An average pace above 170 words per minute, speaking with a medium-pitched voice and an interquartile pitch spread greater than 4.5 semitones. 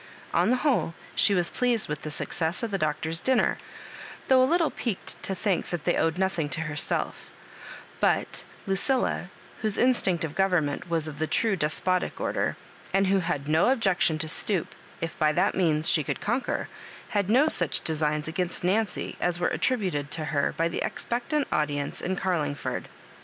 Yes: average, 180 wpm; medium, 175 Hz; average, 5.1 semitones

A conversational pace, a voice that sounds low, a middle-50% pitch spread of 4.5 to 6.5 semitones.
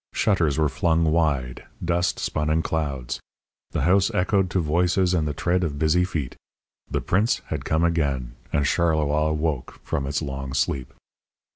No: average, 160 wpm; very low, 80 Hz; average, 3.5 semitones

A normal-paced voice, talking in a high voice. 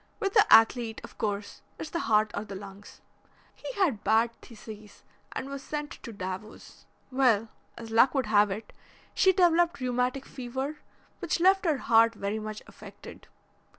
Yes: average, 160 wpm; high, 235 Hz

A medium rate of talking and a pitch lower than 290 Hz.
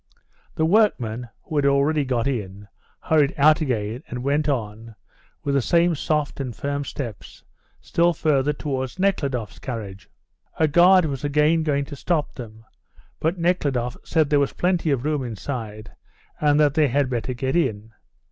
Yes: average, 160 wpm; medium, 140 Hz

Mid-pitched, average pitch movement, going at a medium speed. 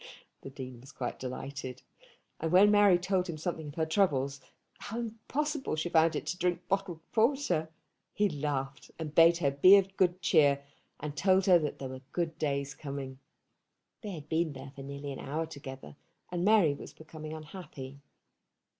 Yes: medium, 160 Hz; average, 4.6 semitones; average, 175 wpm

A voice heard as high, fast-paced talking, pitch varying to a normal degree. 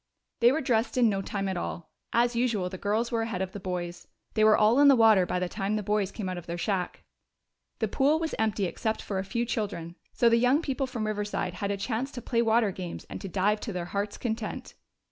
Yes: high, 215 Hz; fast, 245 wpm; average, 3.6 semitones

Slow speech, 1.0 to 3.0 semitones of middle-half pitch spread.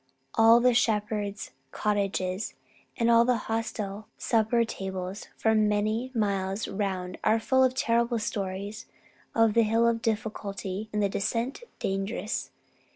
Yes: slow, 125 wpm; narrow, 2.6 semitones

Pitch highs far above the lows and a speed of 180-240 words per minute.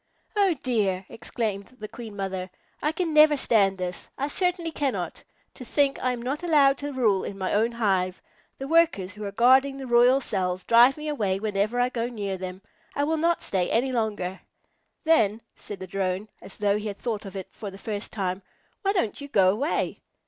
Yes: wide, 5.8 semitones; average, 200 wpm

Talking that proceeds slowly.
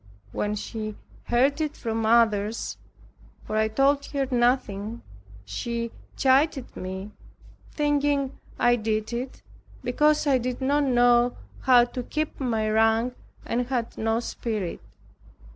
Yes: slow, 125 wpm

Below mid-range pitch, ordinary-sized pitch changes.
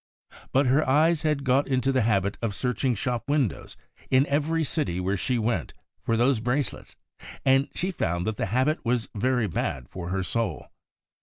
Yes: low, 125 Hz; average, 5.0 semitones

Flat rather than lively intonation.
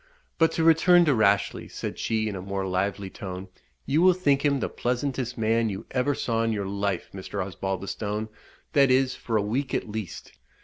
No: wide, 5.5 semitones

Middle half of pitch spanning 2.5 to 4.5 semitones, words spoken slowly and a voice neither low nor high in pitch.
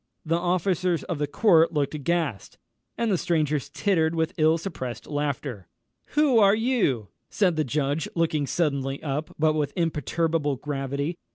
No: average, 3.3 semitones; average, 150 wpm; medium, 155 Hz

